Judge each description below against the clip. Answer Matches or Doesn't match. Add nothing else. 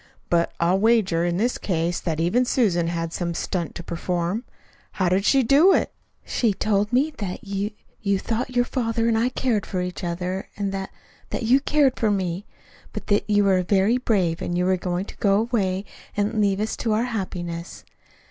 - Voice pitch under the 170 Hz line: Doesn't match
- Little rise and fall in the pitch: Doesn't match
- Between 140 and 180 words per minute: Doesn't match